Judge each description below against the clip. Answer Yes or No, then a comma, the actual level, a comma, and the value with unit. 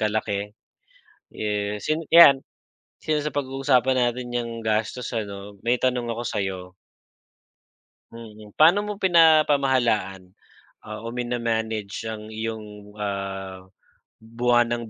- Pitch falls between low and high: No, low, 115 Hz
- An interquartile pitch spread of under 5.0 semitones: Yes, average, 3.6 semitones